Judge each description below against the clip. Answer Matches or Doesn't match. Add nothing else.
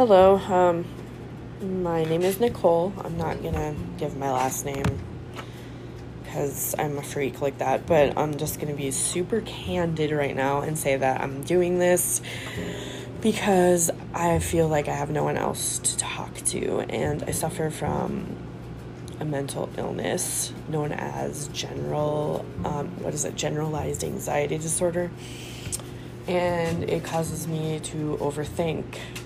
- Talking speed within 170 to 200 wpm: Doesn't match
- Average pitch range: Matches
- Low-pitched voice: Doesn't match